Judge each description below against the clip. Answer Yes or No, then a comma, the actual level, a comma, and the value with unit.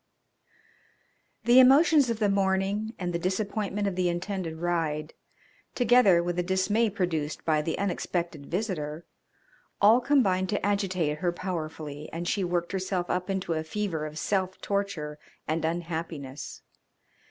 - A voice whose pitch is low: No, medium, 185 Hz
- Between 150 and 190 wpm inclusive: No, average, 140 wpm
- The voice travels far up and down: No, average, 3.7 semitones